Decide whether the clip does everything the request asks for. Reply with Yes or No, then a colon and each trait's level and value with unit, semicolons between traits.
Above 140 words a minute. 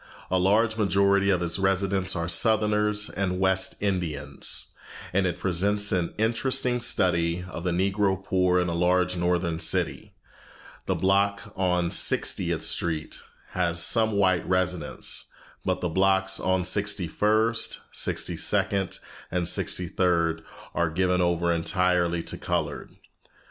No: slow, 135 wpm